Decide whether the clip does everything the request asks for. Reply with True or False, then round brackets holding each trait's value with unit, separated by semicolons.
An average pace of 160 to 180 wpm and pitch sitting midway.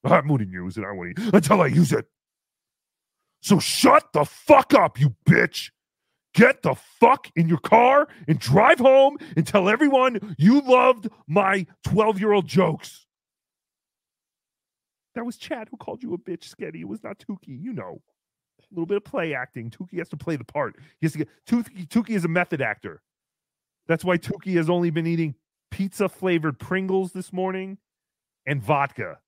True (175 wpm; 180 Hz)